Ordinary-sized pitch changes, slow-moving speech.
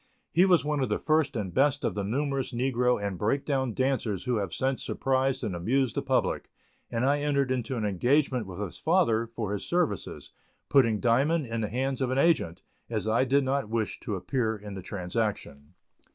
No: average, 4.5 semitones; average, 200 wpm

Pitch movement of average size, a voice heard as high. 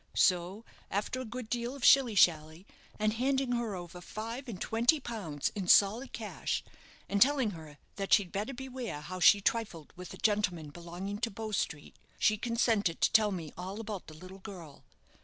Yes: average, 4.7 semitones; high, 205 Hz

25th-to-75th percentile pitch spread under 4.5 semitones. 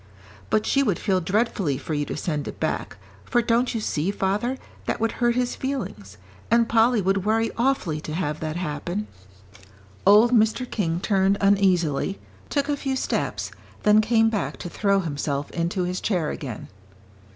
No: wide, 5.6 semitones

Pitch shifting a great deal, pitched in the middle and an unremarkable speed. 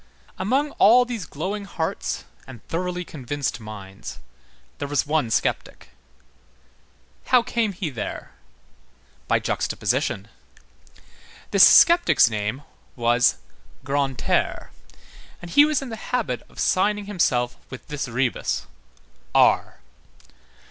No: wide, 9.0 semitones; medium, 155 Hz; slow, 105 wpm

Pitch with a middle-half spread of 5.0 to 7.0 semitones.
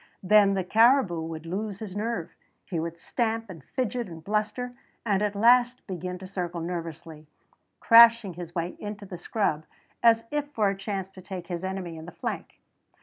No: average, 4.3 semitones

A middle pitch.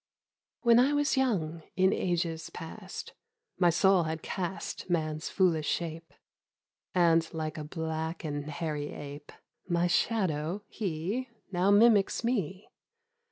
Yes: medium, 170 Hz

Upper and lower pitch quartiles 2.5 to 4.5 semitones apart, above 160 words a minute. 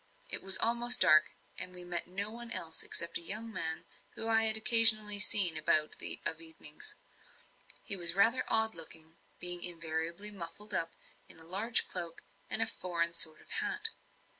No: average, 5.0 semitones; average, 170 wpm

